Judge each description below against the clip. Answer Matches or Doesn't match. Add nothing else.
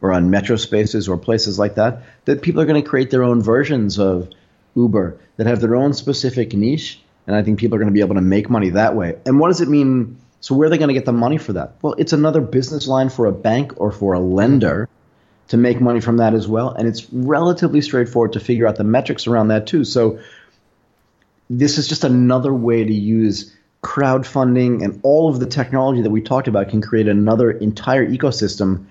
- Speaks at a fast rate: Matches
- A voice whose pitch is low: Matches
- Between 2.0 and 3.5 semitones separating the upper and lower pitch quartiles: Doesn't match